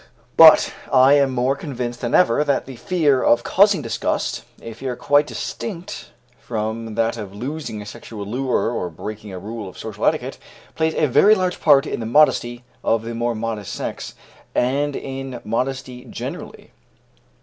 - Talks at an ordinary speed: Yes, average, 165 wpm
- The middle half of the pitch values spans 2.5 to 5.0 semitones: Yes, average, 3.9 semitones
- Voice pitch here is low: Yes, low, 125 Hz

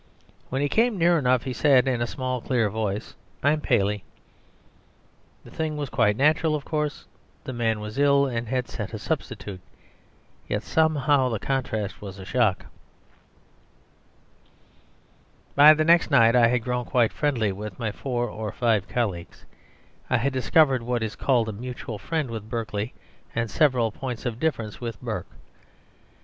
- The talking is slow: No, average, 160 wpm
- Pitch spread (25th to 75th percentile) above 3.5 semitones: Yes, average, 4.1 semitones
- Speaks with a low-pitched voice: Yes, low, 125 Hz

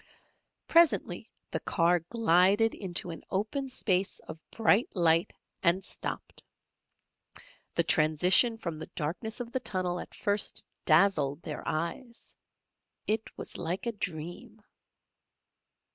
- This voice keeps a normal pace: No, slow, 115 wpm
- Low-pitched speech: No, medium, 185 Hz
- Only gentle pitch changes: No, average, 4.9 semitones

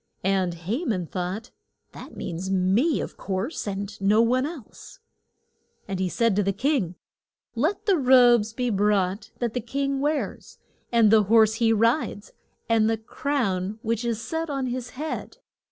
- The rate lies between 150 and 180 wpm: Yes, average, 160 wpm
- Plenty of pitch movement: No, average, 4.5 semitones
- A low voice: No, high, 225 Hz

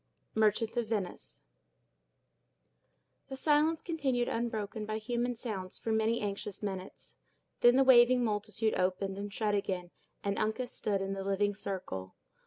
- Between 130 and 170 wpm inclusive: Yes, average, 140 wpm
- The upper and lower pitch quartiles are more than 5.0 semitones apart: No, average, 3.4 semitones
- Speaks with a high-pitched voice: Yes, high, 215 Hz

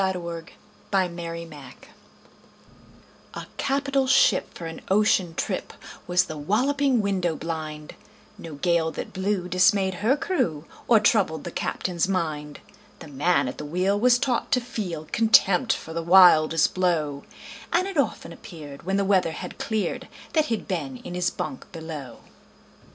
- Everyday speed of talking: Yes, average, 155 wpm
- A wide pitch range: No, average, 4.5 semitones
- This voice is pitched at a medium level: Yes, medium, 180 Hz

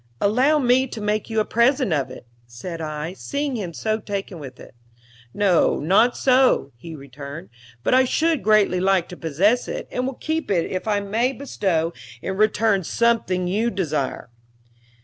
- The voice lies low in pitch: No, high, 200 Hz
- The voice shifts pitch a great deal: Yes, wide, 6.5 semitones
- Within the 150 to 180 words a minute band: Yes, average, 170 wpm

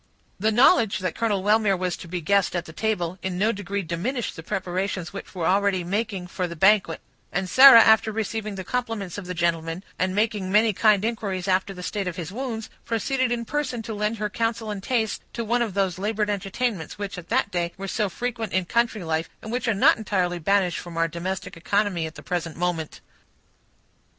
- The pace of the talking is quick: Yes, fast, 210 wpm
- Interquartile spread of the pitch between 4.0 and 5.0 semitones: No, average, 3.6 semitones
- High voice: Yes, high, 200 Hz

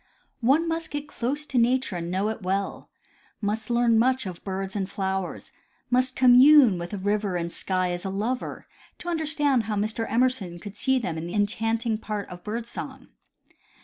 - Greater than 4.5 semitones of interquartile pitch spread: Yes, average, 4.9 semitones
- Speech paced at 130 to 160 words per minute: No, average, 180 wpm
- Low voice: No, high, 220 Hz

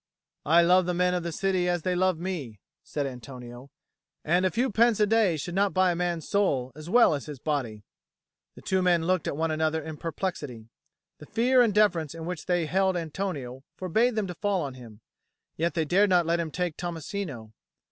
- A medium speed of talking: No, fast, 210 wpm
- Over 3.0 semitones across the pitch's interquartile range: Yes, average, 3.8 semitones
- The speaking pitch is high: No, medium, 175 Hz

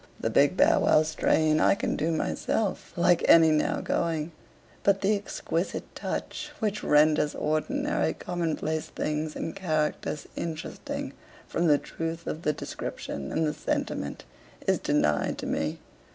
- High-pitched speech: No, medium, 160 Hz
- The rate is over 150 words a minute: No, average, 145 wpm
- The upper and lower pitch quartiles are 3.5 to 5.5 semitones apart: No, narrow, 2.5 semitones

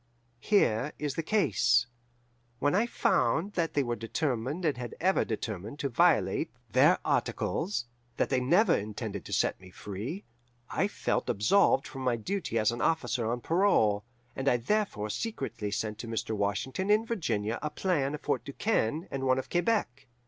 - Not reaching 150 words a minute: No, average, 170 wpm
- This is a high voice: No, low, 135 Hz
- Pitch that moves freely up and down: Yes, wide, 7.5 semitones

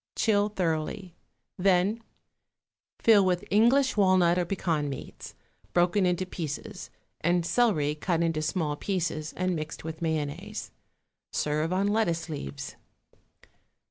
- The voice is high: No, medium, 175 Hz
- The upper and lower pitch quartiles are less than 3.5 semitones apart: No, average, 3.8 semitones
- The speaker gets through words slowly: Yes, slow, 115 wpm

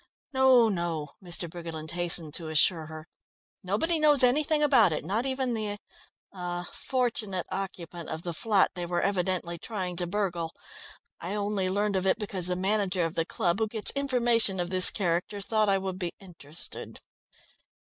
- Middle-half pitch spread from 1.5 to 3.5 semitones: No, average, 3.9 semitones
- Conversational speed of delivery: Yes, average, 165 wpm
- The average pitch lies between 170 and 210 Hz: Yes, high, 190 Hz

